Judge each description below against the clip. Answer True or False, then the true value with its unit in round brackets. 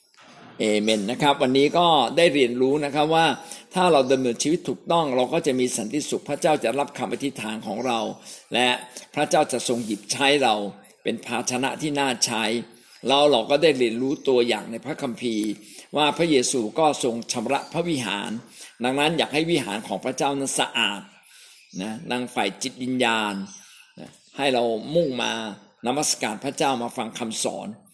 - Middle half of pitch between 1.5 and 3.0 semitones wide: False (3.7 semitones)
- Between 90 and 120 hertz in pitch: False (130 Hz)